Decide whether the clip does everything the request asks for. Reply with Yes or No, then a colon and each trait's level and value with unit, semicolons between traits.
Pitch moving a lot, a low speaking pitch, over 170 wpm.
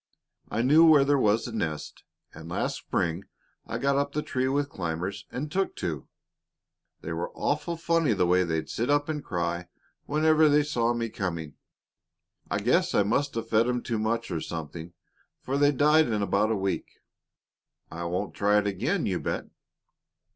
Yes: wide, 7.9 semitones; low, 115 Hz; average, 180 wpm